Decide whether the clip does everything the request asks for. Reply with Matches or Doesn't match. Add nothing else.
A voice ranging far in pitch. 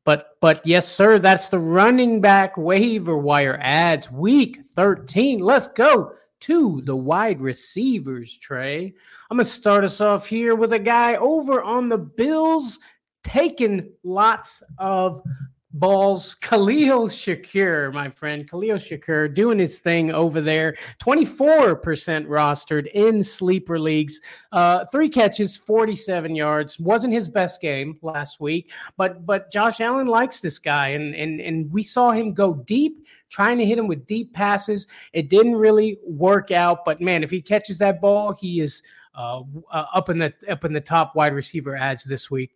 Matches